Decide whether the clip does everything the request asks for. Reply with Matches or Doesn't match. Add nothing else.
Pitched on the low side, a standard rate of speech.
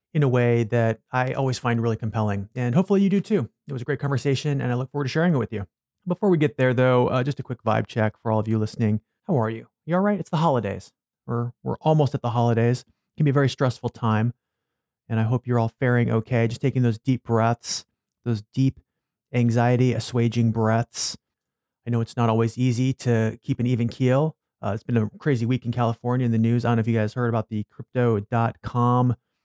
Doesn't match